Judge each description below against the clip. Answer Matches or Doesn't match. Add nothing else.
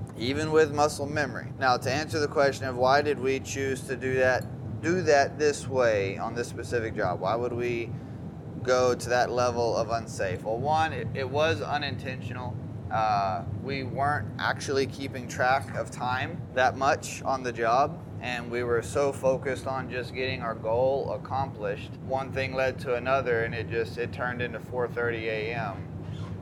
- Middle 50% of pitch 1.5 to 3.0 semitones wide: Matches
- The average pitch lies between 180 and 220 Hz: Doesn't match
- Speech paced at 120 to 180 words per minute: Matches